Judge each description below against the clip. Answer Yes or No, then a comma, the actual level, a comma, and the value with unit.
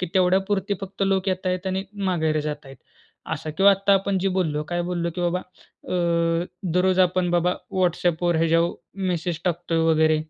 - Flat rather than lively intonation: Yes, narrow, 2.0 semitones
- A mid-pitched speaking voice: Yes, medium, 180 Hz